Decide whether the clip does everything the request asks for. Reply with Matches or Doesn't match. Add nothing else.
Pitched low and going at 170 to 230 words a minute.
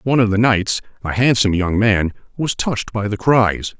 Matches